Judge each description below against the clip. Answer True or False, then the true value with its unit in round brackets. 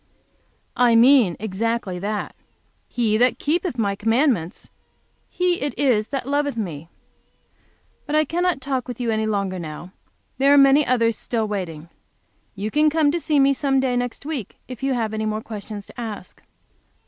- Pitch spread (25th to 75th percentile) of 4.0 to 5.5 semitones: True (4.8 semitones)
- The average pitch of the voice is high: True (235 Hz)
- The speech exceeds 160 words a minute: True (170 wpm)